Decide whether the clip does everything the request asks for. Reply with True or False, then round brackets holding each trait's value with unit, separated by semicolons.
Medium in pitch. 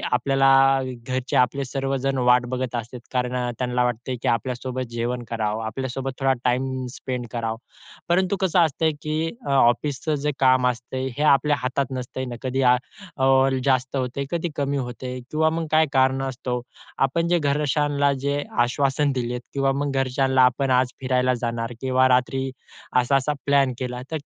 False (130 Hz)